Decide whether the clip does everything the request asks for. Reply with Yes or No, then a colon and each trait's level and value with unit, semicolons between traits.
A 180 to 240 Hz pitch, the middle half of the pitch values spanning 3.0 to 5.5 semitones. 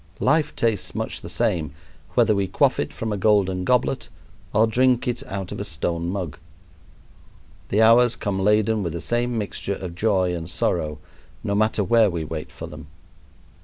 No: low, 100 Hz; average, 4.0 semitones